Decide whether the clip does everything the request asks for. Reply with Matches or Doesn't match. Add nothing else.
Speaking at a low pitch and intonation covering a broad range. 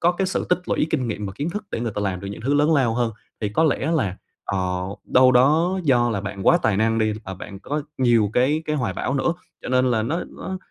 Matches